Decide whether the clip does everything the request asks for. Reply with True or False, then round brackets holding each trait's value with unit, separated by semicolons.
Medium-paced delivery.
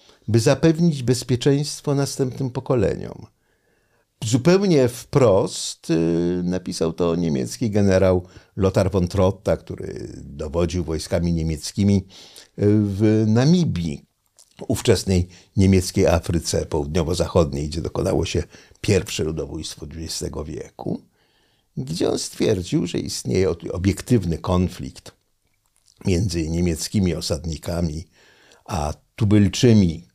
False (85 wpm)